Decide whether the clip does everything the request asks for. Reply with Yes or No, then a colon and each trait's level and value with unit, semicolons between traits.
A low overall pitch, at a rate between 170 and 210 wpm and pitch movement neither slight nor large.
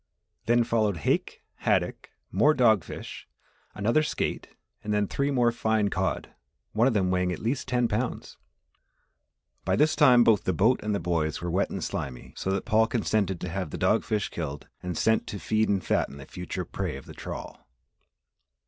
Yes: low, 105 Hz; average, 185 wpm; average, 4.5 semitones